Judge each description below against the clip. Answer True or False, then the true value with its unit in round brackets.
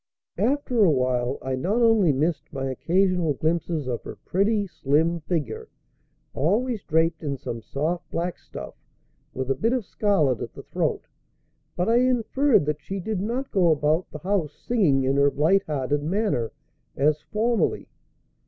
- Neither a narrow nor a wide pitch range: False (6.3 semitones)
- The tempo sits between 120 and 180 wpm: True (160 wpm)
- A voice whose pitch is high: False (165 Hz)